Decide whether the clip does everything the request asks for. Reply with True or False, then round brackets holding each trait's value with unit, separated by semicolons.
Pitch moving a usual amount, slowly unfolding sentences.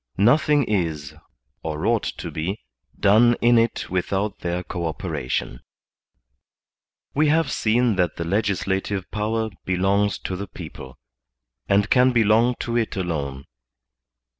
True (4.6 semitones; 125 wpm)